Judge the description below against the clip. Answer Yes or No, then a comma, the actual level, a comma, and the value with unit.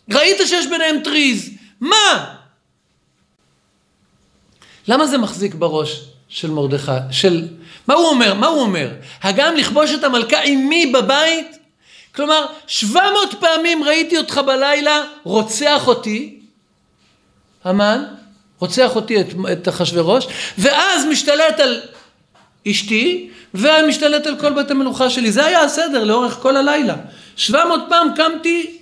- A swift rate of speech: No, average, 120 wpm